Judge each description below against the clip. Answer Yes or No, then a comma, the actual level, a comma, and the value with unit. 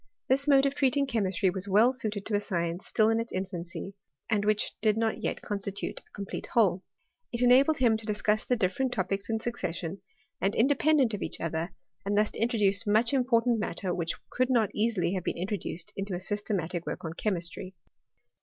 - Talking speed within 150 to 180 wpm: No, average, 195 wpm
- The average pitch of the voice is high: Yes, high, 210 Hz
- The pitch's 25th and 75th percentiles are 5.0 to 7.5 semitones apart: No, average, 3.8 semitones